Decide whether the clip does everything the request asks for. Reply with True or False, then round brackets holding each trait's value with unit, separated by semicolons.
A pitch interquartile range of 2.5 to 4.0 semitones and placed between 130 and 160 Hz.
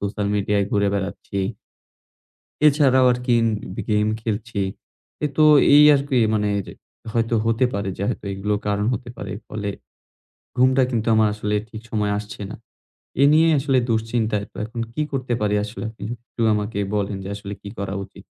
False (3.1 semitones; 110 Hz)